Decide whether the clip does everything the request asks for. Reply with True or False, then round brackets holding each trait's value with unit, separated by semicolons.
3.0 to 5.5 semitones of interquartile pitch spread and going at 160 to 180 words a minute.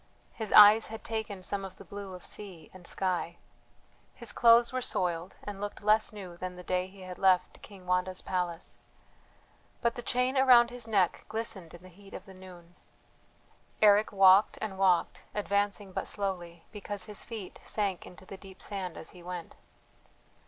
False (2.6 semitones; 175 wpm)